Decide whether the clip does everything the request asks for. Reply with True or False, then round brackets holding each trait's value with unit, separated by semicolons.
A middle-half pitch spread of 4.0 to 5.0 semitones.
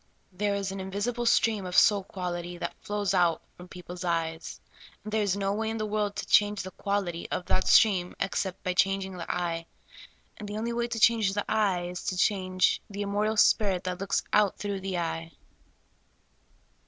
False (2.5 semitones)